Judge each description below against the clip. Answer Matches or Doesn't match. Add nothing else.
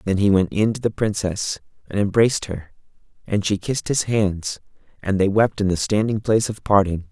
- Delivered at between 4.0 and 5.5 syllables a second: Matches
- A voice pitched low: Matches